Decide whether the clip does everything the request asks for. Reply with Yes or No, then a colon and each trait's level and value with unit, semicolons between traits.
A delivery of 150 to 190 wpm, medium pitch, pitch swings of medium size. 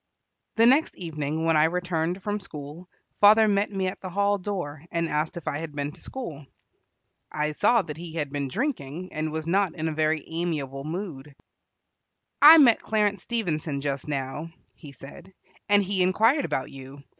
Yes: average, 180 wpm; medium, 165 Hz; average, 5.0 semitones